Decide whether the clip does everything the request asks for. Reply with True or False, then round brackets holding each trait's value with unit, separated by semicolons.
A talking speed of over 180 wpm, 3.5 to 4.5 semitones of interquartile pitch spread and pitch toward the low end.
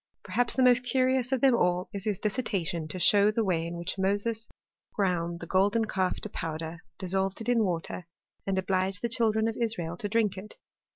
False (195 wpm; 4.0 semitones; 200 Hz)